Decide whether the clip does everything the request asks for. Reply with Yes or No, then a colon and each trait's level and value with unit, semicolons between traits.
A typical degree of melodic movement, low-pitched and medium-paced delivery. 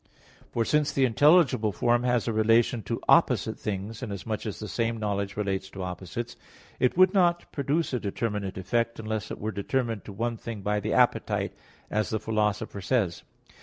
Yes: average, 3.0 semitones; low, 110 Hz; average, 180 wpm